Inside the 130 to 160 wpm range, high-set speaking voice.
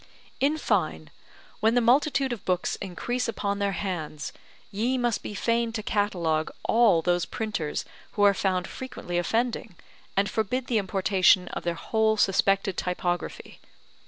Yes: average, 145 wpm; high, 200 Hz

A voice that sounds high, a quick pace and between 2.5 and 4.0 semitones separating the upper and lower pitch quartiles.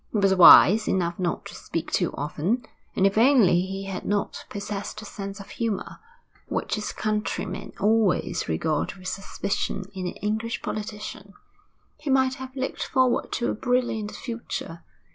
No: high, 205 Hz; average, 160 wpm; average, 3.2 semitones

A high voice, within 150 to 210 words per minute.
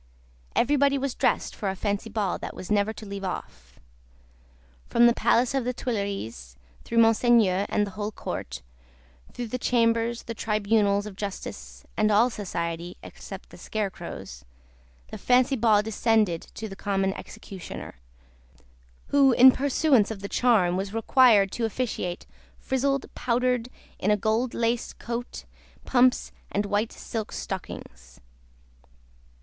No: high, 215 Hz; average, 140 wpm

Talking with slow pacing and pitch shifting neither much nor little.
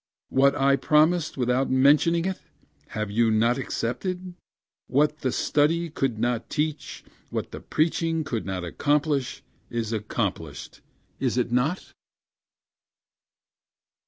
Yes: slow, 115 wpm; average, 4.6 semitones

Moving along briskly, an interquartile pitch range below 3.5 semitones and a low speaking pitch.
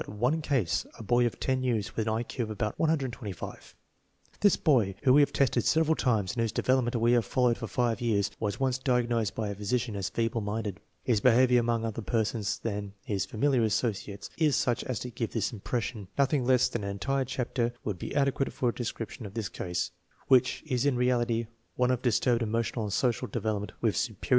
Yes: fast, 215 wpm; average, 3.0 semitones; low, 115 Hz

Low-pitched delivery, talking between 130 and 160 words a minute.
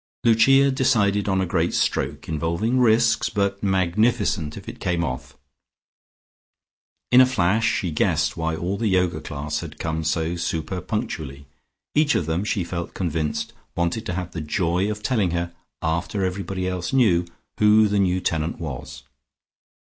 Yes: very low, 90 Hz; average, 155 wpm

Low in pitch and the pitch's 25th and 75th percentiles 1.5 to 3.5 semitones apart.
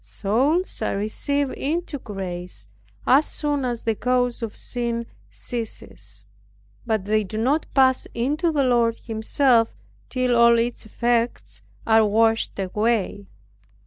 No: high, 235 Hz; average, 3.1 semitones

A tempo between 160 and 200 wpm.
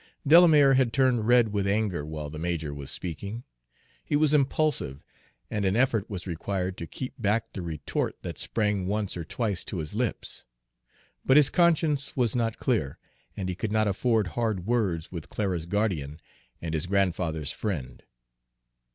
Yes: average, 165 wpm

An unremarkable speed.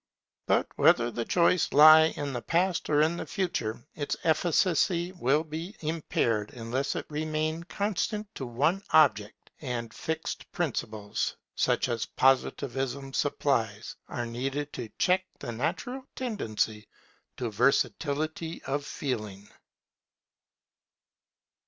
No: slow, 115 wpm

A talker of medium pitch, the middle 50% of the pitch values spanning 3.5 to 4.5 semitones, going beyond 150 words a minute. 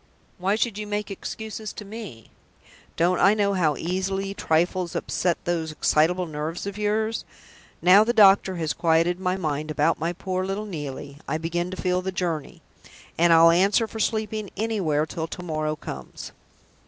Yes: medium, 180 Hz; average, 3.8 semitones; average, 165 wpm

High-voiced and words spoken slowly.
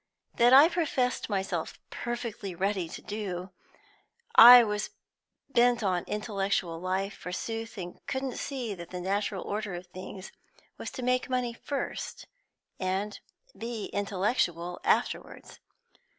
Yes: high, 205 Hz; slow, 120 wpm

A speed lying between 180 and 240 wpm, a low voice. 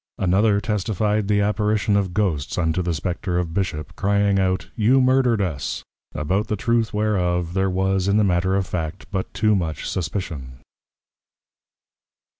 No: average, 150 wpm; very low, 95 Hz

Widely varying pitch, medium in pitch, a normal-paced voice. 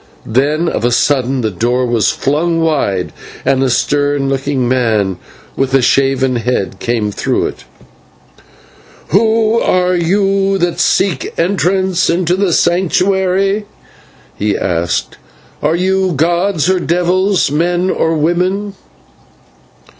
No: wide, 6.3 semitones; medium, 165 Hz; slow, 120 wpm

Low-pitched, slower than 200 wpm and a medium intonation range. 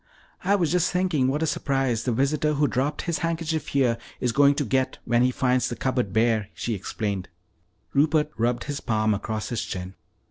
Yes: low, 130 Hz; average, 190 wpm; average, 4.7 semitones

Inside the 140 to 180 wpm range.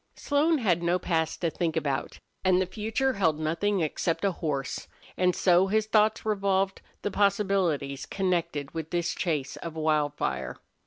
Yes: average, 155 wpm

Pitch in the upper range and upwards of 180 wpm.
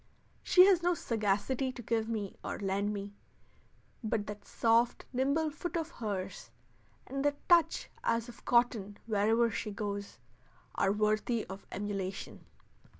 No: high, 225 Hz; average, 140 wpm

